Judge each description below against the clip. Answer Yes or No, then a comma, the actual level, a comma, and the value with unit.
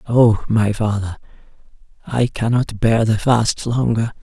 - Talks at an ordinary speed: No, slow, 130 wpm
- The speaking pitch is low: Yes, low, 110 Hz